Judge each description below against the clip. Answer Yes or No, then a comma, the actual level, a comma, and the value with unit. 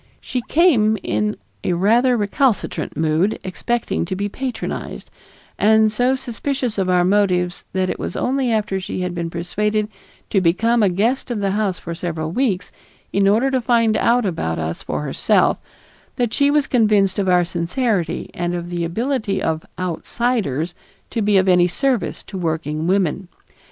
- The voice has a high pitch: Yes, high, 200 Hz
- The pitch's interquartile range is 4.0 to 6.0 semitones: Yes, average, 4.9 semitones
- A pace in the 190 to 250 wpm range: No, average, 165 wpm